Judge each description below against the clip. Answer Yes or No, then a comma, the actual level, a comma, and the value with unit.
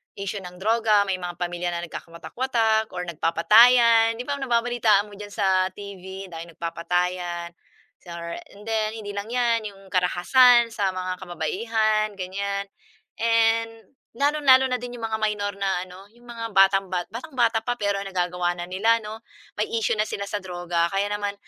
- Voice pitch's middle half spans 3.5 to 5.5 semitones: Yes, average, 3.8 semitones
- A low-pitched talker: No, high, 205 Hz